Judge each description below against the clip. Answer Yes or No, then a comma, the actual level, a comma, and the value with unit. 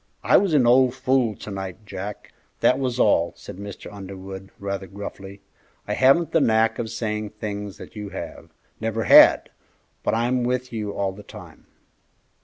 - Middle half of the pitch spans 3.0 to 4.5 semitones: Yes, average, 3.8 semitones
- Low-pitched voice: Yes, low, 105 Hz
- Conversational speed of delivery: Yes, average, 170 wpm